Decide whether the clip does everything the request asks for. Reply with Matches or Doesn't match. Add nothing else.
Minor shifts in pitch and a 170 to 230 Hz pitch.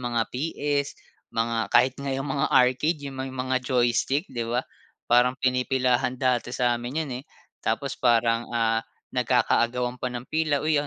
Doesn't match